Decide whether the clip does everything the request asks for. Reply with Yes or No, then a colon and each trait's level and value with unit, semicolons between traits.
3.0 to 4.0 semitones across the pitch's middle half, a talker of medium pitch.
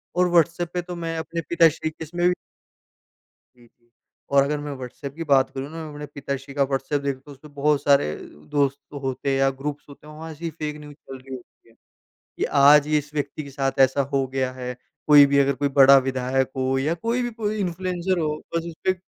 Yes: average, 3.3 semitones; medium, 145 Hz